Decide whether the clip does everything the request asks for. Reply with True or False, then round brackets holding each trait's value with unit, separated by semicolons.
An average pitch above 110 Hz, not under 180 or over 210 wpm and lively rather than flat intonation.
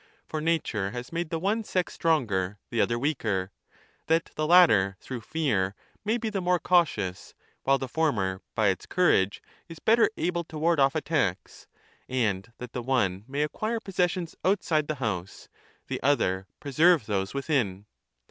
False (140 Hz; 165 wpm; 8.5 semitones)